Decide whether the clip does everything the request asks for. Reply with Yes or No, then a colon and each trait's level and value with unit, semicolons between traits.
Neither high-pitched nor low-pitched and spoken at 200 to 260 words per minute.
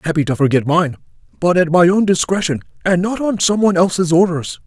Yes: medium, 170 Hz; fast, 205 wpm